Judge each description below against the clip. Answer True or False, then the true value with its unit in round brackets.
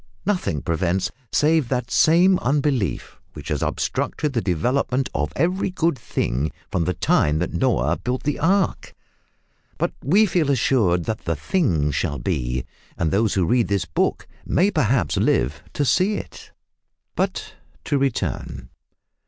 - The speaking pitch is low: True (125 Hz)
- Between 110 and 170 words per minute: True (145 wpm)